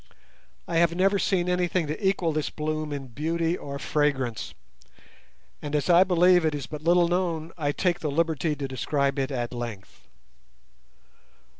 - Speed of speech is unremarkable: Yes, average, 160 wpm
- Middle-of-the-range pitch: Yes, medium, 155 Hz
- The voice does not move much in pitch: No, average, 3.6 semitones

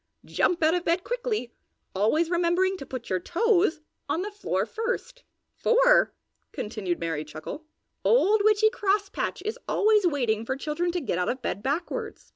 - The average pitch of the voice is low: No, very high, 345 Hz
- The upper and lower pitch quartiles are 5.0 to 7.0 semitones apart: No, wide, 8.7 semitones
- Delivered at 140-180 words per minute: Yes, average, 160 wpm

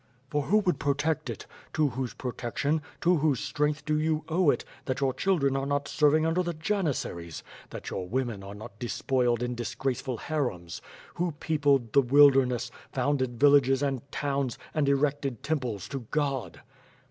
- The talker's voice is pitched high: No, medium, 140 Hz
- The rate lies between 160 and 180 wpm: Yes, average, 165 wpm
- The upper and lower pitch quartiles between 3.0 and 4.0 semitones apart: Yes, average, 3.4 semitones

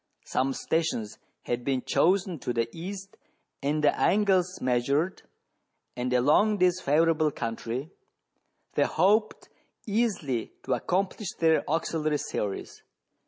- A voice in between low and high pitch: Yes, medium, 160 Hz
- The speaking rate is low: Yes, slow, 115 wpm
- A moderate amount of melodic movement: No, wide, 6.4 semitones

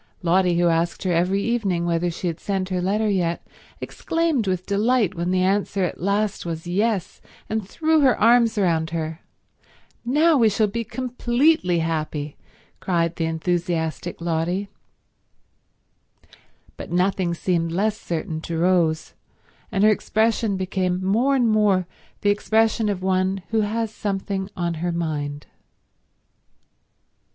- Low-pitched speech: No, high, 190 Hz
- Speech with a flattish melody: No, average, 4.0 semitones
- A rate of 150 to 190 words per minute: No, average, 140 wpm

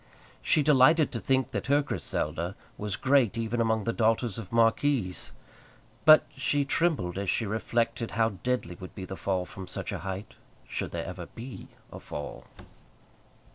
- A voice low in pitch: Yes, low, 115 Hz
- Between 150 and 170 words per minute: Yes, average, 165 wpm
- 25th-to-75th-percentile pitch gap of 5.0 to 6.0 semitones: Yes, average, 5.3 semitones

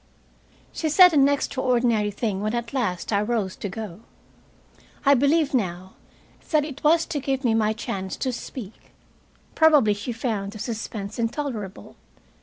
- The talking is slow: No, average, 150 wpm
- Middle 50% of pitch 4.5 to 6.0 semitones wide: Yes, average, 5.1 semitones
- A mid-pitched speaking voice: No, high, 235 Hz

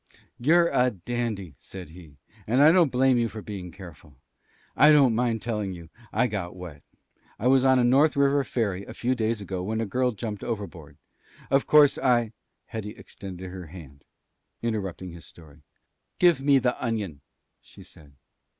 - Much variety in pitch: Yes, wide, 5.7 semitones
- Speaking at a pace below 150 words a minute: No, average, 175 wpm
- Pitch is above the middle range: No, low, 110 Hz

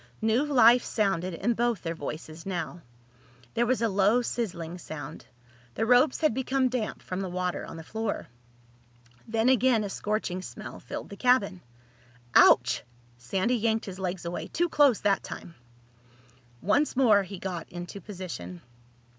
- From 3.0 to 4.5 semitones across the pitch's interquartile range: No, average, 5.1 semitones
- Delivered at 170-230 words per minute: No, average, 155 wpm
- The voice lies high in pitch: Yes, high, 205 Hz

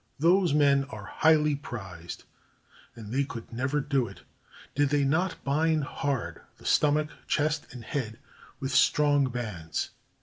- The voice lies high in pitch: No, medium, 140 Hz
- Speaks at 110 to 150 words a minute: Yes, average, 140 wpm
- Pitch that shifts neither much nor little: Yes, average, 3.9 semitones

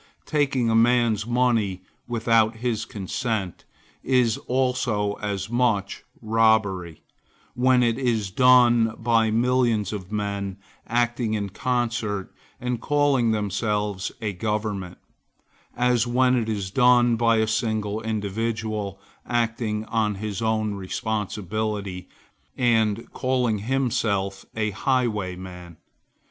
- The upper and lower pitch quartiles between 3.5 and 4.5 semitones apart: No, average, 2.8 semitones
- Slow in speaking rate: Yes, slow, 105 wpm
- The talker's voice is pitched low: Yes, low, 110 Hz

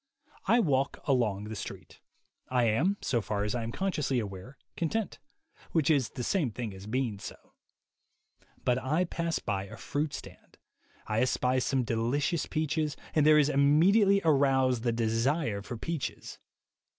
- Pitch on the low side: Yes, low, 130 Hz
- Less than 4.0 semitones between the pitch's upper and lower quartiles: No, average, 5.1 semitones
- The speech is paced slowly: No, average, 150 wpm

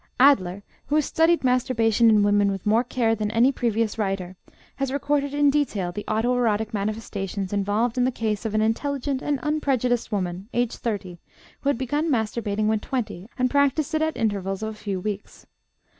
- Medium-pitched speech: No, high, 225 Hz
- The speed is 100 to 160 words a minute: No, average, 185 wpm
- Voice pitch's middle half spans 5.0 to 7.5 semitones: No, average, 4.3 semitones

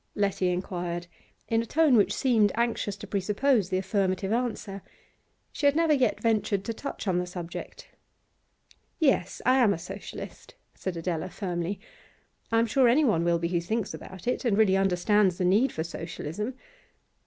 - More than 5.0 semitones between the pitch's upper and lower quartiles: No, average, 4.4 semitones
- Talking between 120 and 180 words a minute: Yes, average, 165 wpm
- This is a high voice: Yes, high, 200 Hz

